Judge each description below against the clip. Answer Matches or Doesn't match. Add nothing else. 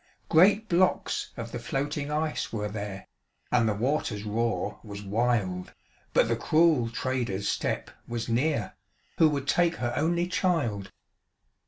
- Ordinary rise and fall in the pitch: Doesn't match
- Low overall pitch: Matches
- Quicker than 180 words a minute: Doesn't match